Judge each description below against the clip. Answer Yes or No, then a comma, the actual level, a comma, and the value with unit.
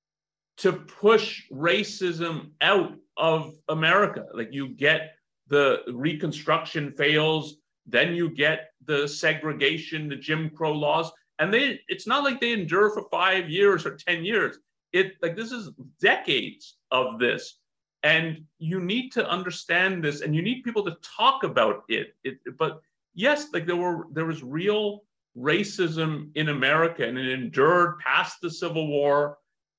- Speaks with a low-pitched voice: No, medium, 165 Hz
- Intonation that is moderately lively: Yes, average, 4.2 semitones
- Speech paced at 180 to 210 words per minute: No, average, 150 wpm